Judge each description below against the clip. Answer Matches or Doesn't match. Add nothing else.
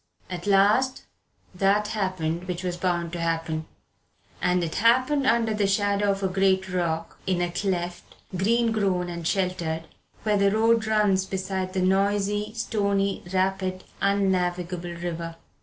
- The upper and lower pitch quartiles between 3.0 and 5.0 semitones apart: Doesn't match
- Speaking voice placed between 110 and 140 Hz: Doesn't match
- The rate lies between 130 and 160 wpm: Matches